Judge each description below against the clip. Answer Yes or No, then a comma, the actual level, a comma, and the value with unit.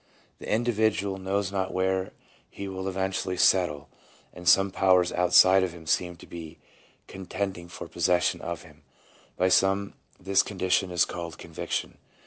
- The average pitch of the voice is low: Yes, very low, 95 Hz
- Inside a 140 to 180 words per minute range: Yes, average, 145 wpm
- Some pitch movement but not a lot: No, narrow, 1.5 semitones